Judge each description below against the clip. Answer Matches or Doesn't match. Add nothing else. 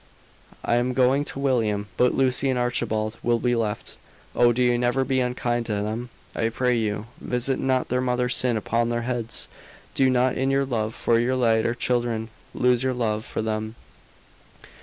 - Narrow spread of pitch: Matches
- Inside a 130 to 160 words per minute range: Doesn't match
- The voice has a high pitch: Doesn't match